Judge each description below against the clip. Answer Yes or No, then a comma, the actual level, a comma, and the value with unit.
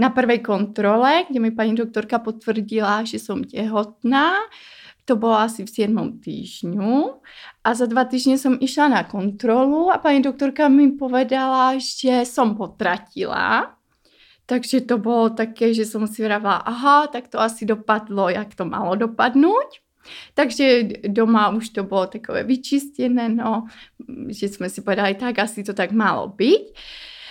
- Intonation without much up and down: No, average, 3.6 semitones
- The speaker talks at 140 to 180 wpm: Yes, average, 150 wpm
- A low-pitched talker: No, high, 230 Hz